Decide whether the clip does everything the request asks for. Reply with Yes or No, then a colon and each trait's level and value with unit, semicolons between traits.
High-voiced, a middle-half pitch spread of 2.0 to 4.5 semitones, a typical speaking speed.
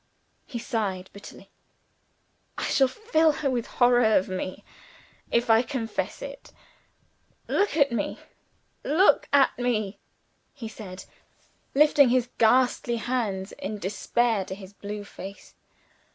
No: high, 235 Hz; average, 4.2 semitones; slow, 125 wpm